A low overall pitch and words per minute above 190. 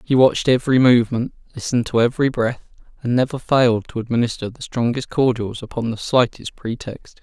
No: low, 120 Hz; average, 165 wpm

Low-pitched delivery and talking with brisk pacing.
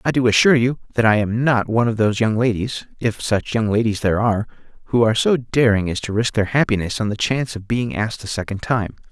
Yes: low, 115 Hz; fast, 245 wpm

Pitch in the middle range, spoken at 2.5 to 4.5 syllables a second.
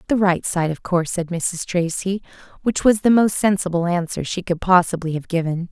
No: medium, 180 Hz; 5.3 syllables/s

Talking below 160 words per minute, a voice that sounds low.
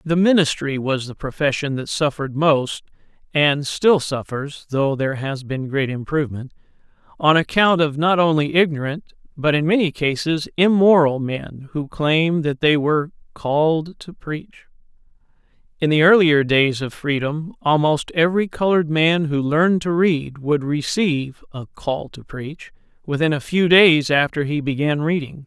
No: average, 150 wpm; medium, 150 Hz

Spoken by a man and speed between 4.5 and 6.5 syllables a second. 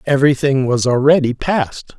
Yes: male; 4.9 syllables/s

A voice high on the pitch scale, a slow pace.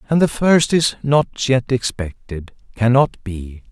No: low, 125 Hz; slow, 130 wpm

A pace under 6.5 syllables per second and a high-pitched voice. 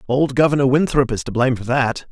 No: 6.3 syllables/s; low, 130 Hz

